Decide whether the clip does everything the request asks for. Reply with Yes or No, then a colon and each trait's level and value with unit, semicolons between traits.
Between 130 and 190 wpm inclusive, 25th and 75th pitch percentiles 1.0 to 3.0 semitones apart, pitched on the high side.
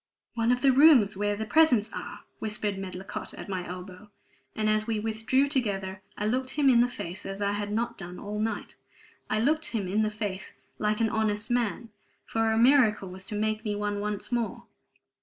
No: average, 200 wpm; narrow, 2.4 semitones; high, 215 Hz